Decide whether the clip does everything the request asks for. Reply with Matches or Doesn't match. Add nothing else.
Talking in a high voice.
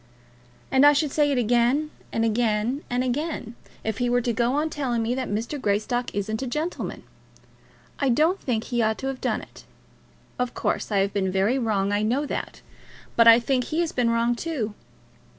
Matches